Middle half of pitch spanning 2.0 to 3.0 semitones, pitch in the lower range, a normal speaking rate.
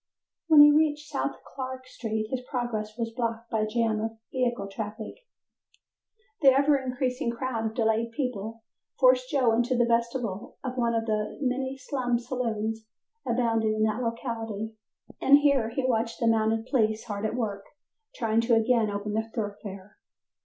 No: narrow, 2.6 semitones; high, 230 Hz; average, 160 wpm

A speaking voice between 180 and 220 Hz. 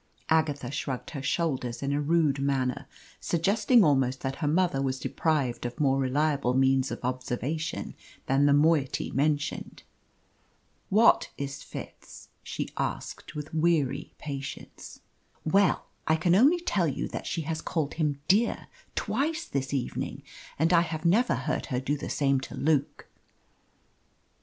No: medium, 145 Hz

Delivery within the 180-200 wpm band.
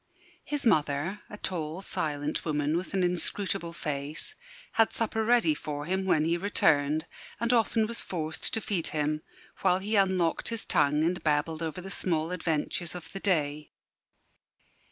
No: average, 155 wpm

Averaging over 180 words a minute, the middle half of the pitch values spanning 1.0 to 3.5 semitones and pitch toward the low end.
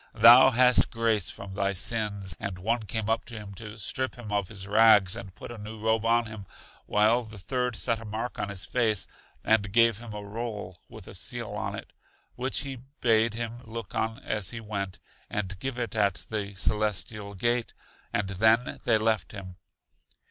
Yes: average, 190 wpm; narrow, 2.4 semitones; low, 110 Hz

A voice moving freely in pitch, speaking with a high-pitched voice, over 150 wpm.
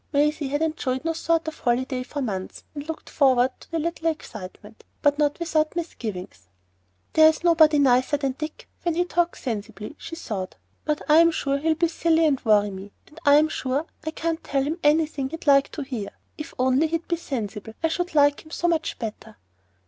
No: average, 4.1 semitones; very high, 295 Hz; average, 195 wpm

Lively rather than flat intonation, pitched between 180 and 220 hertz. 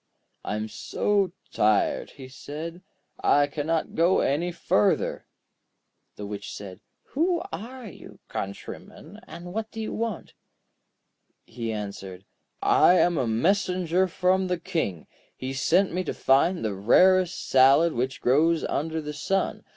No: wide, 6.7 semitones; medium, 165 Hz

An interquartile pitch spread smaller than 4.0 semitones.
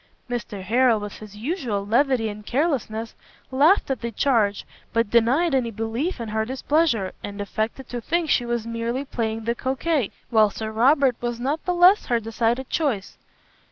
Yes: average, 3.6 semitones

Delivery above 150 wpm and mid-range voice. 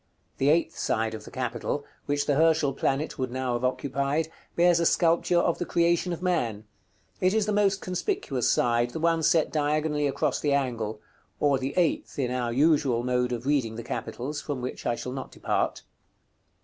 Yes: average, 190 wpm; medium, 145 Hz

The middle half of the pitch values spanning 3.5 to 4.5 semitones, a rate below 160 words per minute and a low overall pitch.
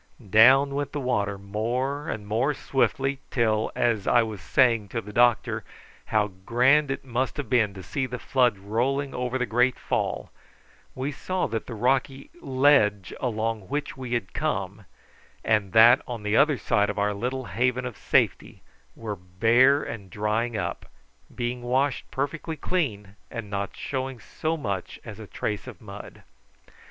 No: average, 4.0 semitones; average, 165 wpm; low, 120 Hz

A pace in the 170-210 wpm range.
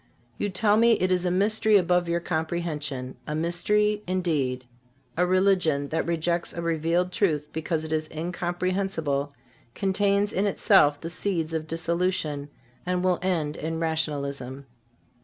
No: average, 140 wpm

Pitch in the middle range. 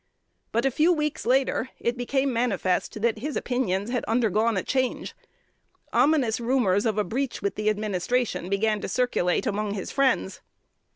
No: high, 230 Hz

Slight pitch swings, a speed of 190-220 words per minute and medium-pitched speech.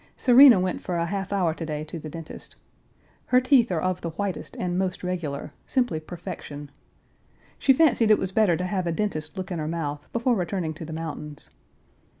No: average, 4.2 semitones; average, 195 wpm; medium, 180 Hz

